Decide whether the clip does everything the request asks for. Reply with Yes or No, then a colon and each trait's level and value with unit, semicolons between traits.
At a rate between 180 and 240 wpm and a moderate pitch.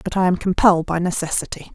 Yes: fast, 205 wpm; medium, 175 Hz